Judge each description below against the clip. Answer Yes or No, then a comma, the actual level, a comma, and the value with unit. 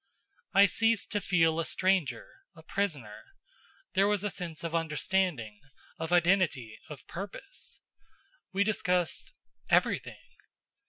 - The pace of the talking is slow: Yes, slow, 115 wpm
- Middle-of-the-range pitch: Yes, medium, 180 Hz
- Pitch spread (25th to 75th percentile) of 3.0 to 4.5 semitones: Yes, average, 3.7 semitones